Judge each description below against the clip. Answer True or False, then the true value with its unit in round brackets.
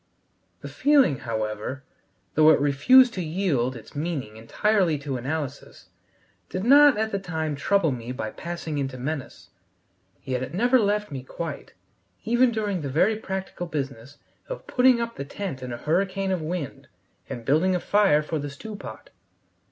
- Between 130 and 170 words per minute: True (165 wpm)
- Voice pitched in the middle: True (160 Hz)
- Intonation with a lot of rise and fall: True (6.7 semitones)